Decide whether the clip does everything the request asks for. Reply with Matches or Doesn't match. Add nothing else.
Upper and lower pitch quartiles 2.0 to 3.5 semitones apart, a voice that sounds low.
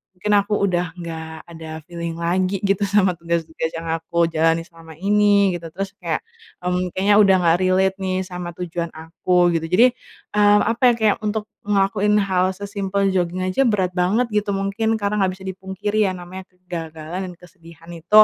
Doesn't match